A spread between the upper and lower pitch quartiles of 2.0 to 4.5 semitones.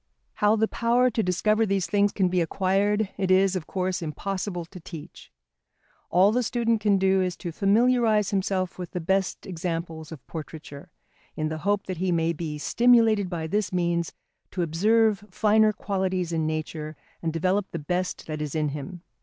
Yes: average, 3.8 semitones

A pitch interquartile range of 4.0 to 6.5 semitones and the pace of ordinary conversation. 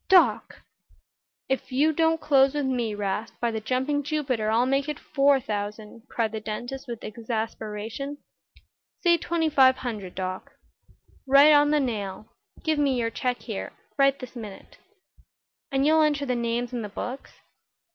Yes: average, 4.5 semitones; average, 155 wpm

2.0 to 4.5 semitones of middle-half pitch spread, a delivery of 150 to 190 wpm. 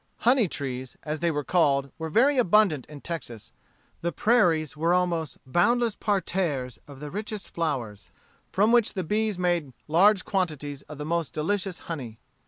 No: wide, 5.4 semitones; average, 160 wpm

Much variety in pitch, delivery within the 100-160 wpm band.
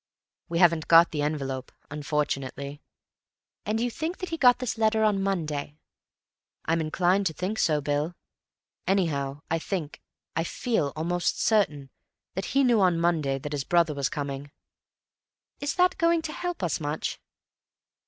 Yes: wide, 6.6 semitones; average, 145 wpm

